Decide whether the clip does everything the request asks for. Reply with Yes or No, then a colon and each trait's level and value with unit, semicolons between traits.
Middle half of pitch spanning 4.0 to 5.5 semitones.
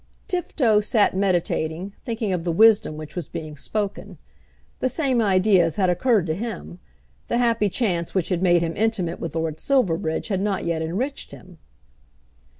Yes: average, 5.1 semitones